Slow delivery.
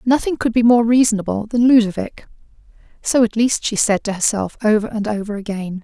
No: average, 185 wpm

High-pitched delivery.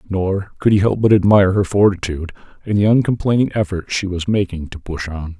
No: very low, 95 Hz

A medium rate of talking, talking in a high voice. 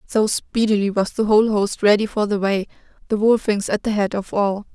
No: fast, 215 wpm; high, 210 Hz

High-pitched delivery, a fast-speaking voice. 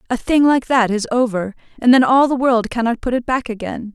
Yes: high, 240 Hz; fast, 245 wpm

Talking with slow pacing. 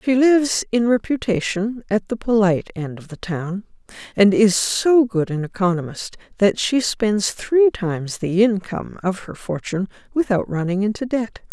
No: average, 160 wpm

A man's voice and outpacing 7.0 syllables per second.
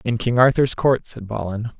No: male; 4.8 syllables/s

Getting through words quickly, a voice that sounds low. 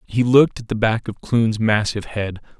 Yes: fast, 210 wpm; low, 110 Hz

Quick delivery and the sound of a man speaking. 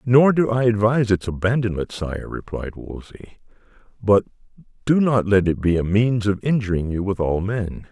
No: average, 175 wpm; male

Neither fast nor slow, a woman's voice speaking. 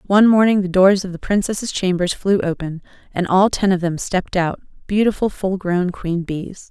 Yes: average, 195 wpm; female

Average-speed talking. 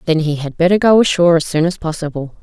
No: fast, 245 wpm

